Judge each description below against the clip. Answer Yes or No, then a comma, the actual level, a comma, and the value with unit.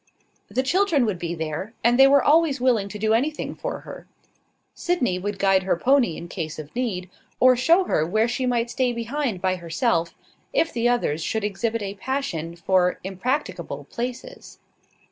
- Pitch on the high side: Yes, high, 230 Hz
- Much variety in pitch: Yes, wide, 5.9 semitones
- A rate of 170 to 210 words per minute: Yes, average, 175 wpm